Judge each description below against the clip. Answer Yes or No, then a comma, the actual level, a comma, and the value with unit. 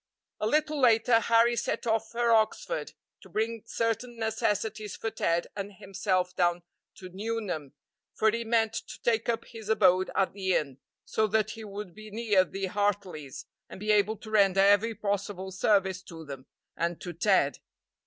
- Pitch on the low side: No, high, 210 Hz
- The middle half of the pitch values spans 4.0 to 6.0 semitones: No, average, 3.1 semitones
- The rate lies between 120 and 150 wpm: No, average, 170 wpm